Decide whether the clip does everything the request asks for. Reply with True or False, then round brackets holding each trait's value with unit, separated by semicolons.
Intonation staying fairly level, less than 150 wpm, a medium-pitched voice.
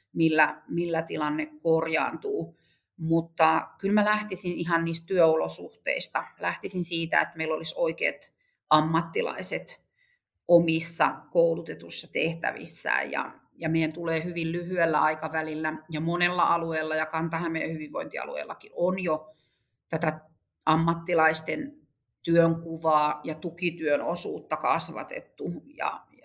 True (1.6 semitones; 100 wpm; 165 Hz)